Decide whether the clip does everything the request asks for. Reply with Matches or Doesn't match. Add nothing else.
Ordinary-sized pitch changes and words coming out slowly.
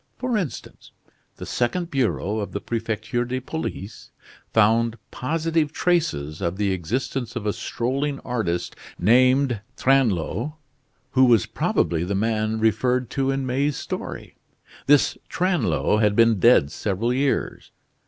Matches